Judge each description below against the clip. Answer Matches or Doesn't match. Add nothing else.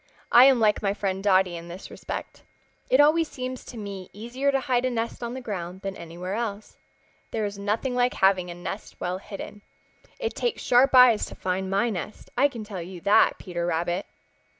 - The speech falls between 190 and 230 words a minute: Matches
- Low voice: Doesn't match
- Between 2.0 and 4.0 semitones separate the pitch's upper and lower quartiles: Doesn't match